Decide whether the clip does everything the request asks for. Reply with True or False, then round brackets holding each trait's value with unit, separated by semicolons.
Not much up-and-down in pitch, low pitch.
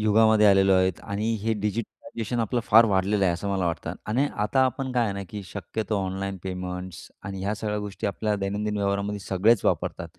True (2.1 semitones; 105 Hz)